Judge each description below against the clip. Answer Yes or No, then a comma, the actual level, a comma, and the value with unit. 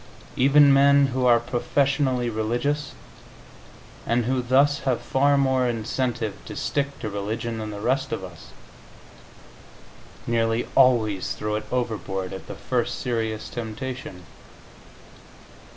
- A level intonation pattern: No, average, 3.5 semitones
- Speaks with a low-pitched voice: Yes, low, 120 Hz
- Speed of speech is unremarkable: No, slow, 120 wpm